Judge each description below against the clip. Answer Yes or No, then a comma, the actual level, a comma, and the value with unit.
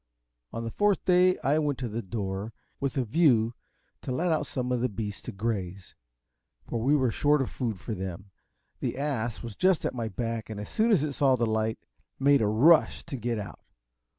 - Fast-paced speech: Yes, fast, 210 wpm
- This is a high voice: No, low, 120 Hz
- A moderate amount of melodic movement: Yes, average, 4.8 semitones